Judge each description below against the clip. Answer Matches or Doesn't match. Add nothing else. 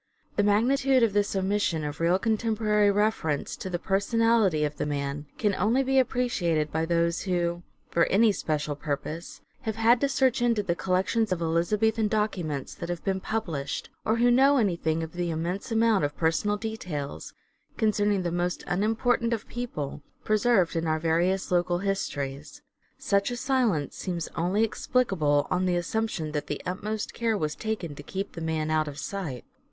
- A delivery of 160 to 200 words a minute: Matches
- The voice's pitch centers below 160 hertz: Doesn't match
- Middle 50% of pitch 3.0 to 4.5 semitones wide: Doesn't match